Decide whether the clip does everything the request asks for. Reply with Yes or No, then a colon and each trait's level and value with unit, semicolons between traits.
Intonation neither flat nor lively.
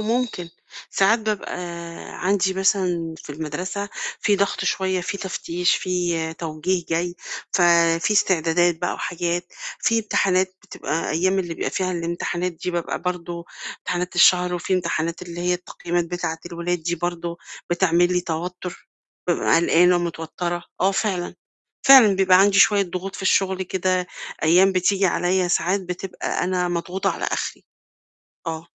No: narrow, 1.8 semitones